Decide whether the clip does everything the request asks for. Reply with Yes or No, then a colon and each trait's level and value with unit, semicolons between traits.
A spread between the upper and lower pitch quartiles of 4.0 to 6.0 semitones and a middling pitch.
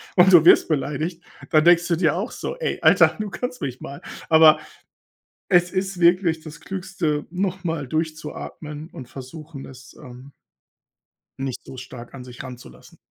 Yes: average, 4.5 semitones; medium, 160 Hz